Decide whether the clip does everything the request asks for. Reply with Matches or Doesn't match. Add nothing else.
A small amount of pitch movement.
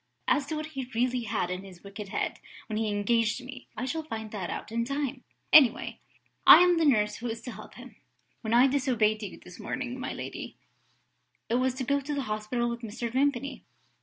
Doesn't match